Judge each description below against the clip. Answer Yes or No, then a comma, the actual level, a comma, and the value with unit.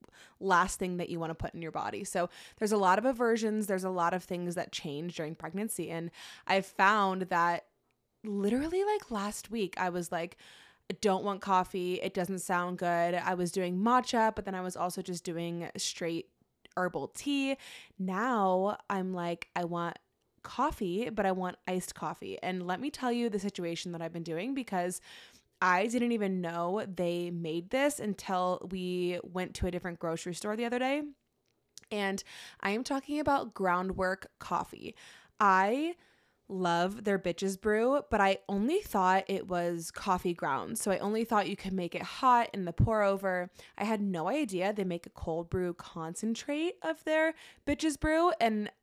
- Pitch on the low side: No, high, 190 Hz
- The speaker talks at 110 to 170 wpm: No, average, 180 wpm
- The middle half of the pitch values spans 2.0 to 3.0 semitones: No, average, 3.7 semitones